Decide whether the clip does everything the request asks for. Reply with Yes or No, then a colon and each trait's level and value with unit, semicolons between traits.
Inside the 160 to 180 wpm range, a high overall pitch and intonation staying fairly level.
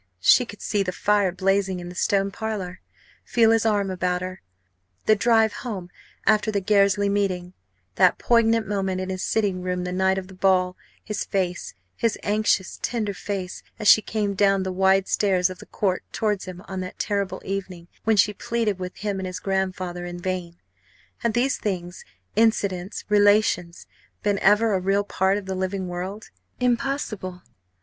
Yes: average, 175 wpm; high, 195 Hz; narrow, 2.2 semitones